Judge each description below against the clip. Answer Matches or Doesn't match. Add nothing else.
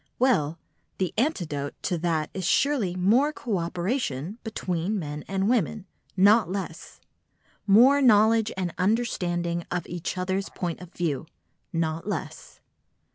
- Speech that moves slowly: Matches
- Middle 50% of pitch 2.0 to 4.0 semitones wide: Doesn't match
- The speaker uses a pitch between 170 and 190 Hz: Matches